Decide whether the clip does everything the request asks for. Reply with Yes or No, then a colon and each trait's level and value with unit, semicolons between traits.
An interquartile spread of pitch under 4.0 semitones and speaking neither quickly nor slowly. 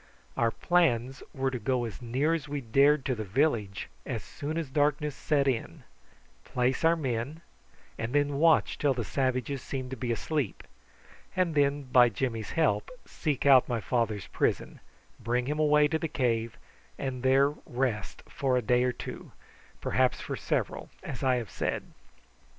Yes: average, 3.4 semitones; average, 165 wpm